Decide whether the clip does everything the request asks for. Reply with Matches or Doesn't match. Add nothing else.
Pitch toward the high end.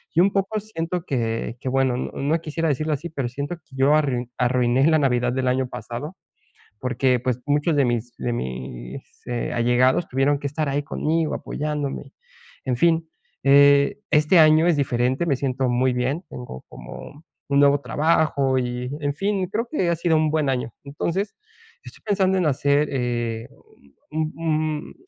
Doesn't match